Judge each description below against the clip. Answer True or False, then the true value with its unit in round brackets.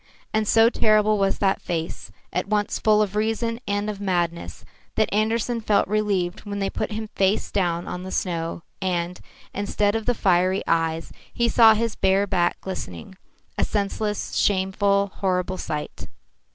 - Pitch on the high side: True (200 Hz)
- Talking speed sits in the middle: True (160 wpm)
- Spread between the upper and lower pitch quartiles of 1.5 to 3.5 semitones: True (2.7 semitones)